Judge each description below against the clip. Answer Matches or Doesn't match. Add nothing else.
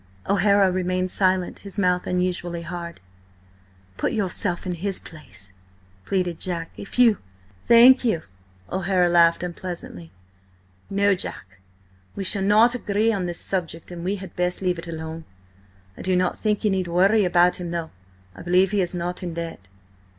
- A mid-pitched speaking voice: Matches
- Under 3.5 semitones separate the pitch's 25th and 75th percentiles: Matches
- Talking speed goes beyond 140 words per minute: Matches